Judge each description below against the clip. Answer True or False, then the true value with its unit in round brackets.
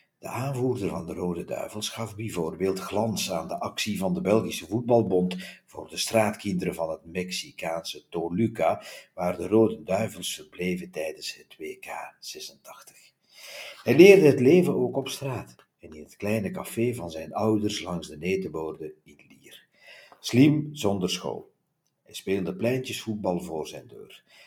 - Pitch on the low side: True (105 Hz)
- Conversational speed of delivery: True (150 wpm)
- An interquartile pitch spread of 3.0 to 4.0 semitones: False (5.6 semitones)